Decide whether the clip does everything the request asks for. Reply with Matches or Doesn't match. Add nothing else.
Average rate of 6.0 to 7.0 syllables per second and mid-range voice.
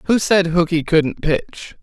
Doesn't match